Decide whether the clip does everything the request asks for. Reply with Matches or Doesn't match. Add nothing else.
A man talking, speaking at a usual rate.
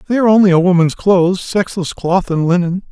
Matches